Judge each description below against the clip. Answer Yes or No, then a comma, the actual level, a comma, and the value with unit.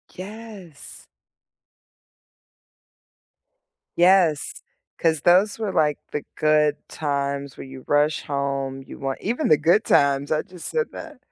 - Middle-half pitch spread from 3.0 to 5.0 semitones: Yes, average, 4.6 semitones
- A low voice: No, medium, 155 Hz